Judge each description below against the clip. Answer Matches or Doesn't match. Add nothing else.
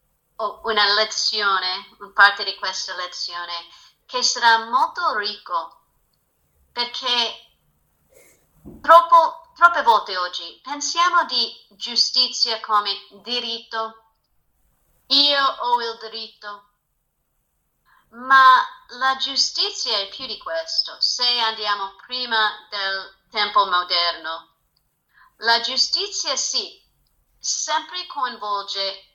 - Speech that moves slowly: Matches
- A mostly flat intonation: Doesn't match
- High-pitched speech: Matches